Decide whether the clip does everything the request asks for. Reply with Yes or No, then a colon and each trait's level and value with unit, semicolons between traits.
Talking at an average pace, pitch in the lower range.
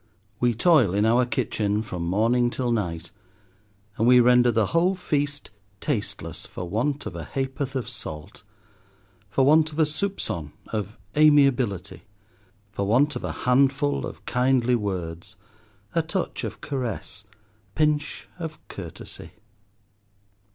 No: slow, 130 wpm; low, 120 Hz